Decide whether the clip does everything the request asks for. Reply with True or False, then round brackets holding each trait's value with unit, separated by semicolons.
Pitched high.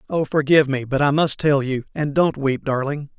False (140 Hz)